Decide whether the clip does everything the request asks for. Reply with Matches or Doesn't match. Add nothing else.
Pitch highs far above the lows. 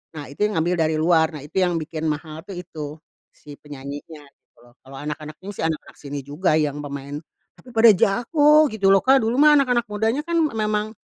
Matches